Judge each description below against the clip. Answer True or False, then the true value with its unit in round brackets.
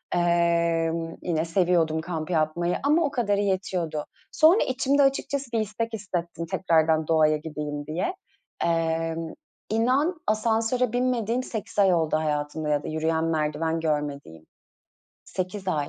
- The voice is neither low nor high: True (170 Hz)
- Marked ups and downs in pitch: True (5.8 semitones)